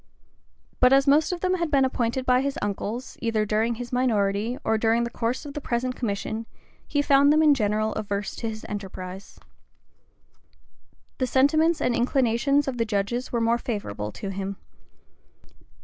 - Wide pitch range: No, average, 4.2 semitones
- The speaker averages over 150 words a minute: Yes, average, 170 wpm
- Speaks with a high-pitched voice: Yes, high, 235 Hz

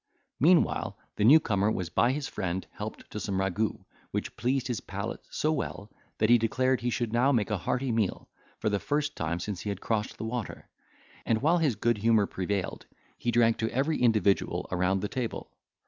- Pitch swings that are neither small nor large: Yes, average, 3.7 semitones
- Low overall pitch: Yes, low, 115 Hz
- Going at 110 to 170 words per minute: No, average, 195 wpm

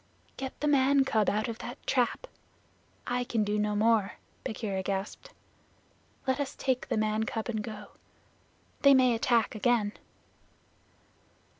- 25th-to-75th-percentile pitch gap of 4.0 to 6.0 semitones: No, average, 3.5 semitones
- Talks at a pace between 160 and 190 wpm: No, average, 140 wpm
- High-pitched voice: Yes, high, 230 Hz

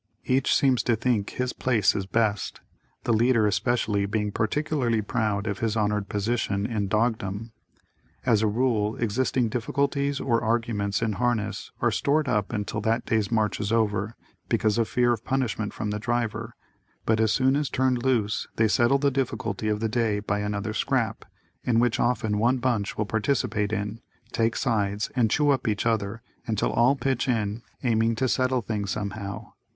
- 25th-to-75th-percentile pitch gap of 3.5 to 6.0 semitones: No, average, 2.8 semitones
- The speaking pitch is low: Yes, low, 110 Hz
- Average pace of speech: Yes, average, 175 wpm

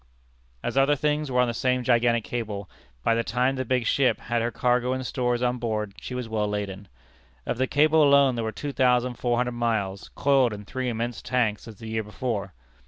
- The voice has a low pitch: Yes, low, 120 Hz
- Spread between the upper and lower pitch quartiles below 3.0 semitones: Yes, narrow, 2.4 semitones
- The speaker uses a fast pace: Yes, fast, 215 wpm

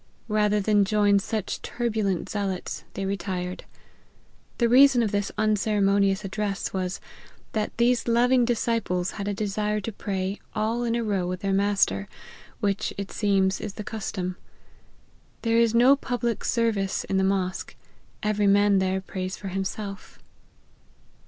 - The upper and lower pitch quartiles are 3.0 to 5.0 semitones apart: No, narrow, 2.4 semitones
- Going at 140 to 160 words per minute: Yes, average, 145 wpm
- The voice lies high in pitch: Yes, high, 205 Hz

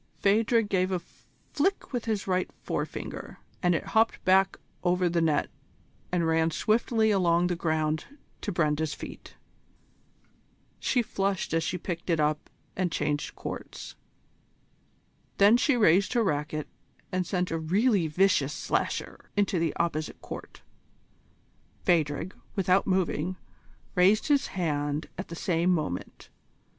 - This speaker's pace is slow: Yes, slow, 130 wpm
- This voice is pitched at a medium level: Yes, medium, 180 Hz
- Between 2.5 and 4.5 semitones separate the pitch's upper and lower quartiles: Yes, average, 3.6 semitones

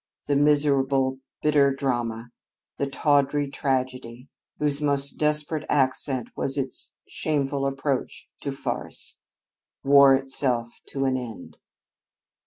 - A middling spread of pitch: No, narrow, 1.6 semitones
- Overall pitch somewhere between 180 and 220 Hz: No, low, 135 Hz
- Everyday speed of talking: No, slow, 105 wpm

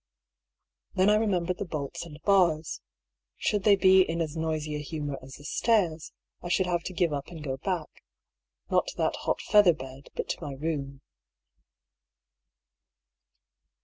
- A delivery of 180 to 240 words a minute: No, average, 165 wpm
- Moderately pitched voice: Yes, medium, 165 Hz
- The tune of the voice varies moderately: Yes, average, 4.0 semitones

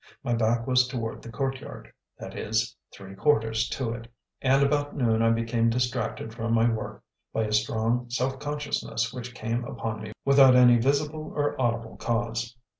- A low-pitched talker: Yes, low, 120 Hz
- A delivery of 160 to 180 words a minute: Yes, average, 170 wpm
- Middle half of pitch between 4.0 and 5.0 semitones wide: No, narrow, 2.6 semitones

